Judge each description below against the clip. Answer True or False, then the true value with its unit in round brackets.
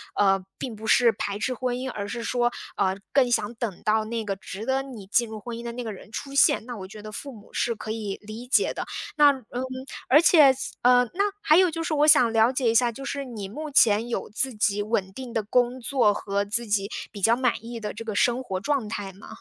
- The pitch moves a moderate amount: True (3.5 semitones)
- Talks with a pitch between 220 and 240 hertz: True (230 Hz)